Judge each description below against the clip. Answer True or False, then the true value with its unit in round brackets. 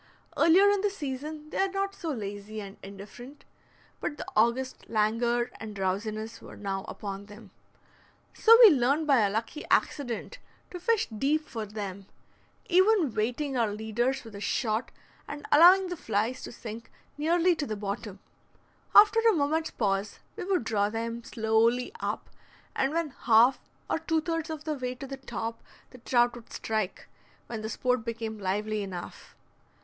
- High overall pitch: True (240 Hz)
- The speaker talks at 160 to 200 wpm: True (165 wpm)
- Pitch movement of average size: False (6.1 semitones)